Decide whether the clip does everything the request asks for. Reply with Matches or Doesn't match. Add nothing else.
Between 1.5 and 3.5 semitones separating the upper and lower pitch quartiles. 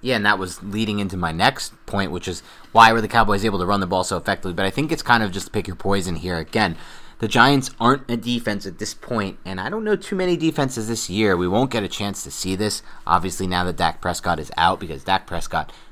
Doesn't match